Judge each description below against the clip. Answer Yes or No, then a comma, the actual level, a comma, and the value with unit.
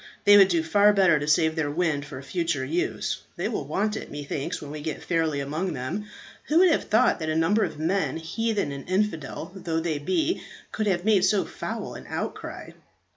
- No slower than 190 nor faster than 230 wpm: Yes, fast, 205 wpm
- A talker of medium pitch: Yes, medium, 165 Hz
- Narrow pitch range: No, average, 5.0 semitones